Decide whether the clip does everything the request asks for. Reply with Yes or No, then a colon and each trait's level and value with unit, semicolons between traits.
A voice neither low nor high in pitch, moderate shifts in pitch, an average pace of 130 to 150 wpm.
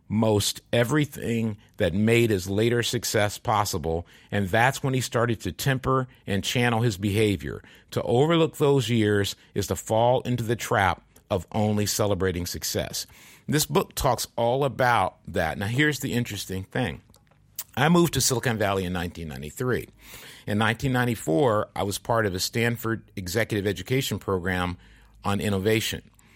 No: low, 110 Hz; average, 3.5 semitones; average, 145 wpm